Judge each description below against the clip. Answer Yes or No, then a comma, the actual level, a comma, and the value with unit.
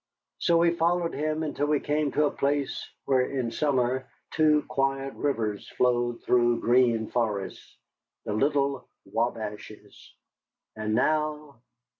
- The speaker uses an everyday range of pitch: Yes, average, 4.0 semitones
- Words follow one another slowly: Yes, slow, 125 wpm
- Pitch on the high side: No, low, 135 Hz